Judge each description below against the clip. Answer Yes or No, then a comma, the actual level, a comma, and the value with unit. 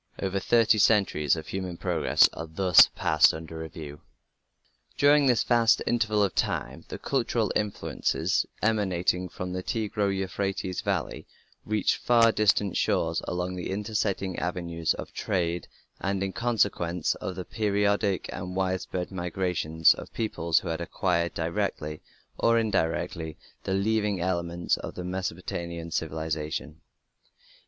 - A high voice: No, very low, 95 Hz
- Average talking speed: No, slow, 130 wpm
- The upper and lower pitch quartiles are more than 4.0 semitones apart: No, average, 3.6 semitones